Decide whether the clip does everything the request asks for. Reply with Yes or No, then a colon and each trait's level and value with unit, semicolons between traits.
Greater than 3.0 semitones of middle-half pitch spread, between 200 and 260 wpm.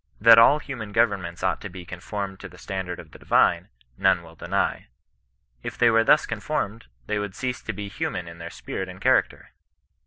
Yes: average, 4.0 semitones; fast, 205 wpm